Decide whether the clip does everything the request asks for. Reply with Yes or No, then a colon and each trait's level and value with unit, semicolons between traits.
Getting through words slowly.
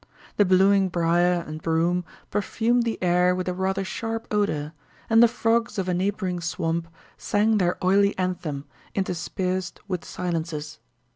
No: average, 145 wpm